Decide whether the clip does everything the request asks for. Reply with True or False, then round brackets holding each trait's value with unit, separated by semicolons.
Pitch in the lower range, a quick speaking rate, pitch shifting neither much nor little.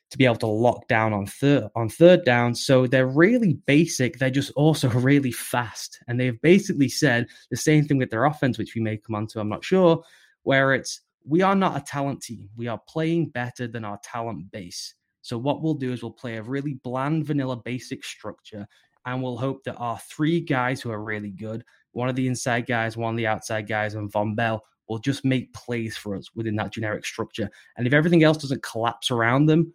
True (125 Hz; 225 wpm; 3.9 semitones)